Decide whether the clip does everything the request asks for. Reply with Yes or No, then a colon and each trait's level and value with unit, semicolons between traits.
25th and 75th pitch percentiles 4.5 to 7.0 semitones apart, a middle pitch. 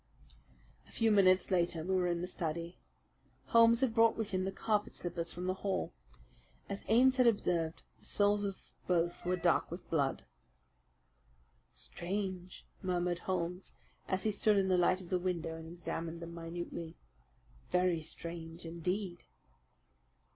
No: narrow, 2.6 semitones; medium, 180 Hz